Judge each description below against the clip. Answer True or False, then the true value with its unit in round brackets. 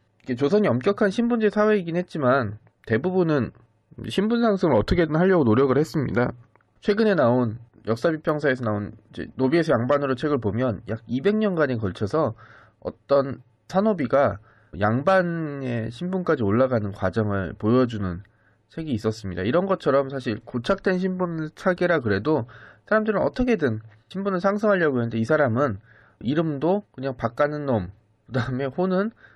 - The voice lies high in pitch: False (135 Hz)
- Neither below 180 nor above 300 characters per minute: False (330 characters per minute)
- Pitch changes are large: True (8.3 semitones)